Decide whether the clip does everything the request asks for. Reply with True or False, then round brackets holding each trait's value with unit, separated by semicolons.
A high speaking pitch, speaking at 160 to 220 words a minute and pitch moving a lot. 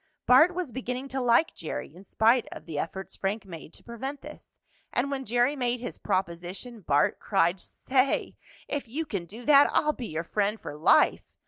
True (235 Hz; 190 wpm; 6.1 semitones)